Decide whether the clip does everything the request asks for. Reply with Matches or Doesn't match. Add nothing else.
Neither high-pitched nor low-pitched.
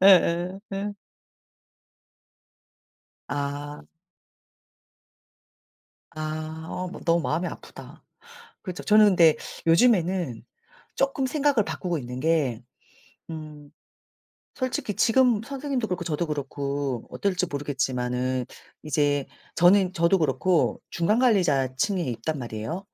Matches